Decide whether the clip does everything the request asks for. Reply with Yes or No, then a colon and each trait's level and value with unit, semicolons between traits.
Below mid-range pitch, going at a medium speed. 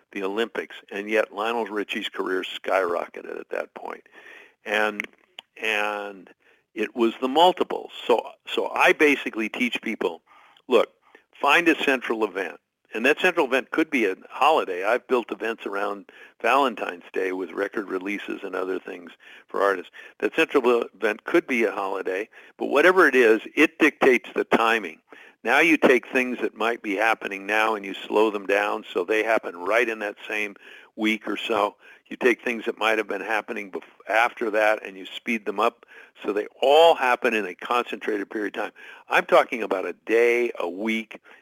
Yes: low, 120 Hz; average, 175 wpm